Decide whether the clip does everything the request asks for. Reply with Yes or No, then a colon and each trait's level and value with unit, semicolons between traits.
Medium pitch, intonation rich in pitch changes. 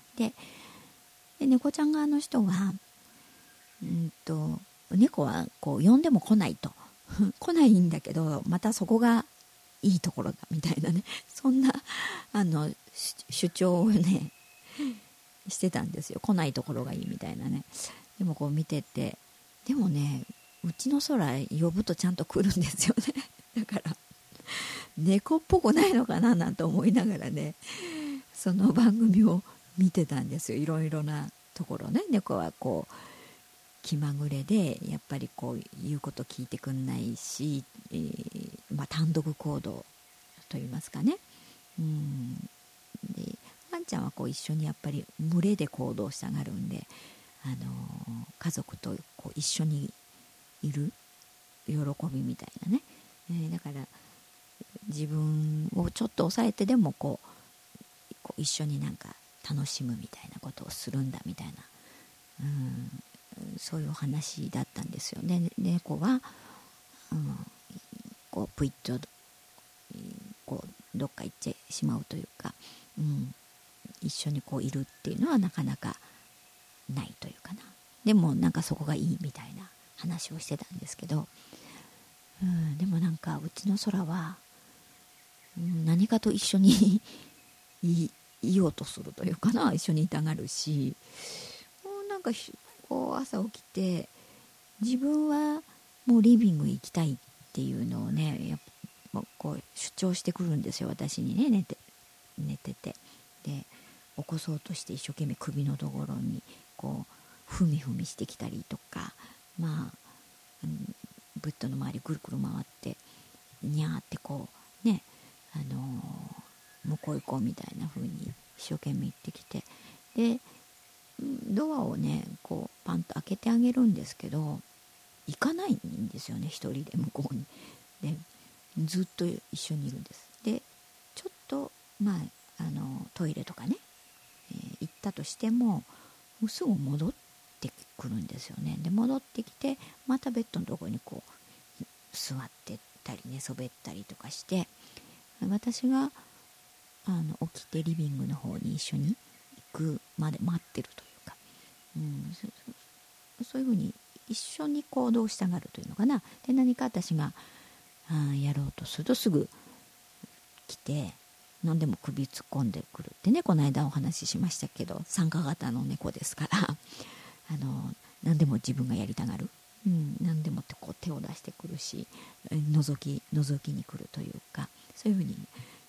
Yes: medium, 175 Hz; wide, 6.7 semitones